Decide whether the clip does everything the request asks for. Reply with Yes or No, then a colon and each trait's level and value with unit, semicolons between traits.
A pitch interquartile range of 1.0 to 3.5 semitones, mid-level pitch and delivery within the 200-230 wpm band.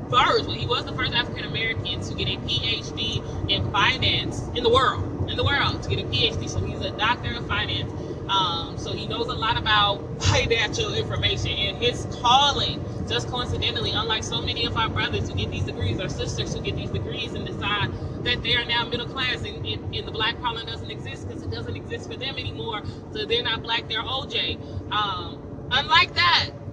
No: average, 2.7 semitones; low, 115 Hz; fast, 205 wpm